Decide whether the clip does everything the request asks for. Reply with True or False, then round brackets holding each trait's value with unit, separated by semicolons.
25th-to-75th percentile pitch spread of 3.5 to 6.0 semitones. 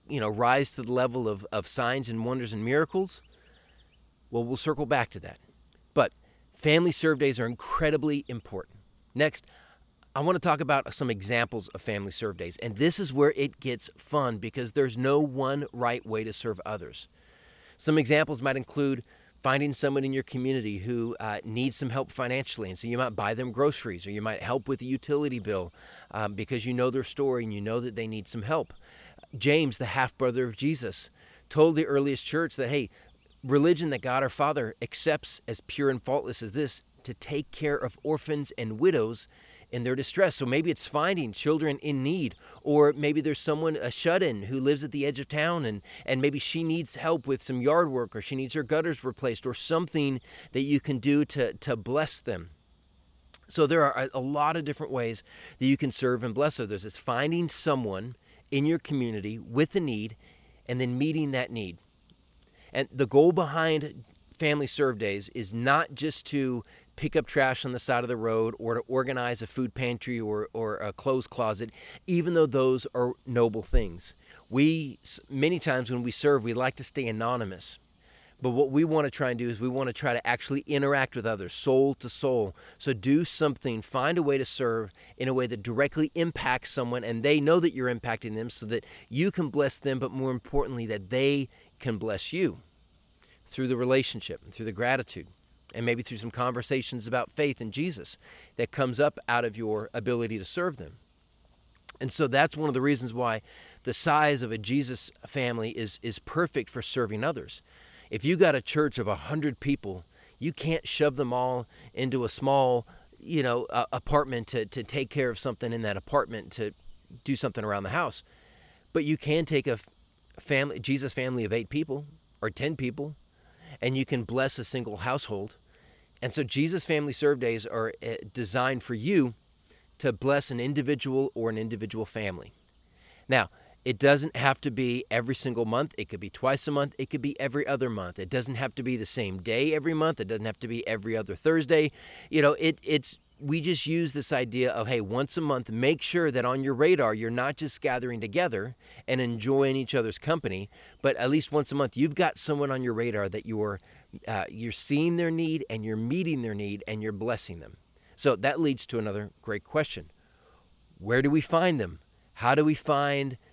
True (4.2 semitones)